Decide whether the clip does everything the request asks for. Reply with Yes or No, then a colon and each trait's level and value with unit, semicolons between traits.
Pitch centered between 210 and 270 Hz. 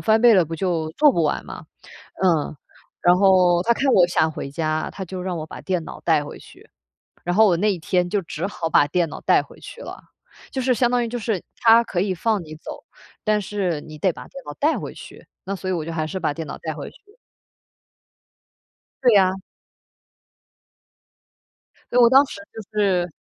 No: medium, 185 Hz